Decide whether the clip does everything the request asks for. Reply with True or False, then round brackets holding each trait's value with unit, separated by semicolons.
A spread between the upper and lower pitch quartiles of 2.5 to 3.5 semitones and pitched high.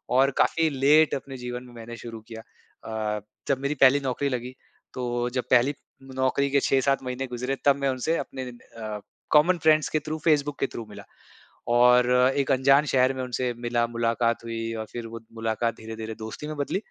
False (2.9 semitones; 125 Hz)